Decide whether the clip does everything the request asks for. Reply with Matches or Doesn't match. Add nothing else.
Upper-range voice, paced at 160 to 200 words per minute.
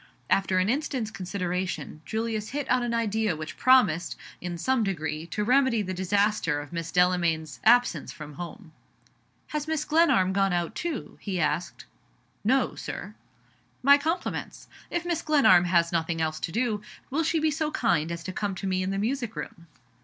Matches